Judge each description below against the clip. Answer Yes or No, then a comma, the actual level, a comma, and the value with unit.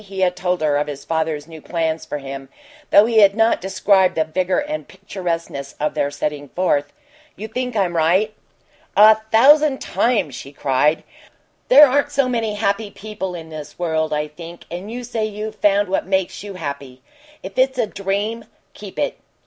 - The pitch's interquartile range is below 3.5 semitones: No, wide, 5.5 semitones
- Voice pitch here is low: No, high, 190 Hz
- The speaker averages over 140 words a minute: Yes, average, 180 wpm